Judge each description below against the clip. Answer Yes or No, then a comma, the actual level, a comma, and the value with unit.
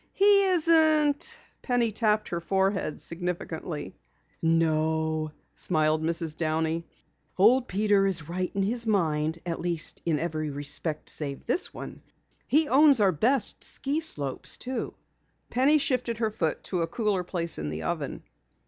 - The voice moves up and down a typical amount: No, wide, 7.2 semitones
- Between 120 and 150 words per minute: Yes, average, 145 wpm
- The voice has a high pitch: No, medium, 180 Hz